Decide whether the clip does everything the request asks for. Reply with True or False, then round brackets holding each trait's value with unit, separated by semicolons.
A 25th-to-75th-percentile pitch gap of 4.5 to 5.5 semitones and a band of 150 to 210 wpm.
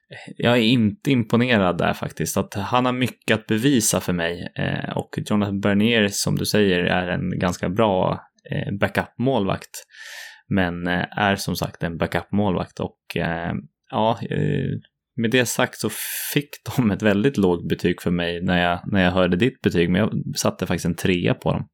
True (4.8 semitones; 180 wpm)